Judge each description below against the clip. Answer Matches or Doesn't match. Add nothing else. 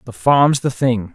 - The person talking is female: Doesn't match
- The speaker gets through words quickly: Matches